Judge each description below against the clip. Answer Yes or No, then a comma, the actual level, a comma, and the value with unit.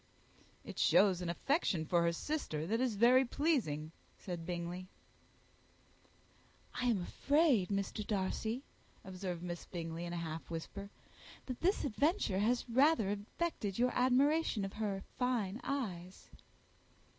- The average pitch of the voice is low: No, high, 200 Hz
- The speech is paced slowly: Yes, slow, 130 wpm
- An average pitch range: No, wide, 6.3 semitones